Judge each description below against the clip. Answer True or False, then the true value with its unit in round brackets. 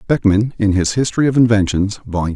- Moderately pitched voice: False (105 Hz)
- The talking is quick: False (180 wpm)